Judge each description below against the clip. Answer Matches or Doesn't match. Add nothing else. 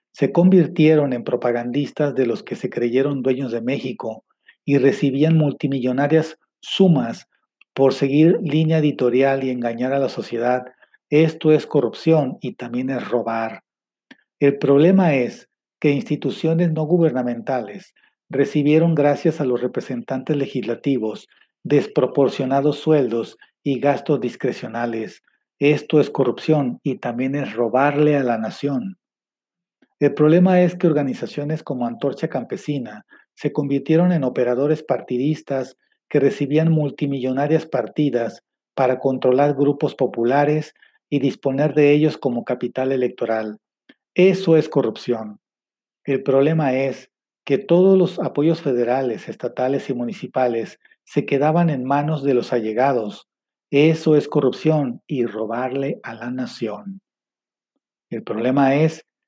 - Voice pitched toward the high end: Doesn't match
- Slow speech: Matches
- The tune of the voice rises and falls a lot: Doesn't match